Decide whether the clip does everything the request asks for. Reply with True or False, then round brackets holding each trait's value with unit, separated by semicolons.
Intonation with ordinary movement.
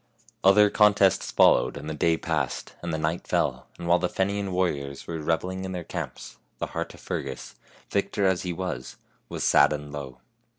True (3.9 semitones)